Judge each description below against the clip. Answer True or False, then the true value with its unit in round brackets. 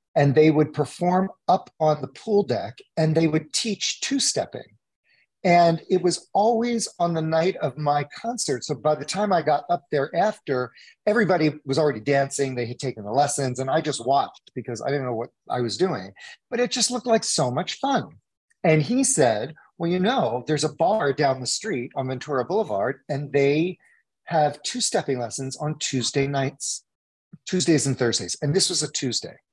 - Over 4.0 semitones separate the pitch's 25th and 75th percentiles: True (4.9 semitones)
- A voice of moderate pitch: True (150 Hz)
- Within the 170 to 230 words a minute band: True (195 wpm)